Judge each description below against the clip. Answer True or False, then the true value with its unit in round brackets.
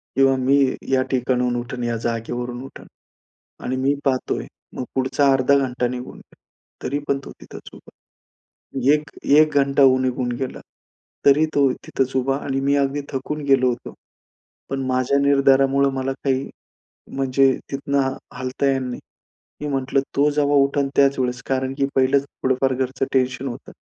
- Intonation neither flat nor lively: False (1.3 semitones)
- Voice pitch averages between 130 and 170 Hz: True (135 Hz)